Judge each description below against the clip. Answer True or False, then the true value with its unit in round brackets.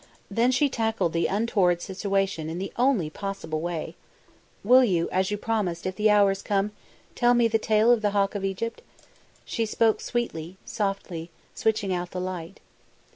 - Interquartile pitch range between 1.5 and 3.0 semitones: False (3.6 semitones)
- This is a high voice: True (200 Hz)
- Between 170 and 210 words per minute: True (175 wpm)